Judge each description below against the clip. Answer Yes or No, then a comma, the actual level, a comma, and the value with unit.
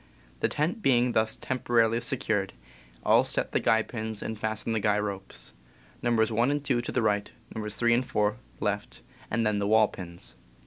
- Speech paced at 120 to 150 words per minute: No, average, 185 wpm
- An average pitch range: No, narrow, 2.3 semitones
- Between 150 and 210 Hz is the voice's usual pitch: No, low, 110 Hz